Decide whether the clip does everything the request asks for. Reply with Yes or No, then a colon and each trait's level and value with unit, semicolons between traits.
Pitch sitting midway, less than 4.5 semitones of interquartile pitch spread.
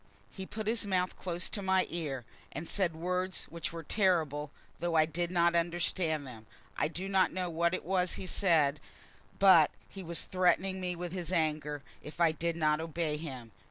Yes: medium, 170 Hz; average, 2.8 semitones